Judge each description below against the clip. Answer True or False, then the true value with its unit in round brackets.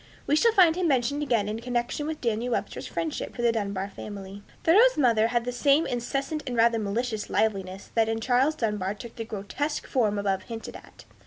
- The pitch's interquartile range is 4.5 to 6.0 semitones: True (4.9 semitones)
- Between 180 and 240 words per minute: True (195 wpm)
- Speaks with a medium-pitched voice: False (235 Hz)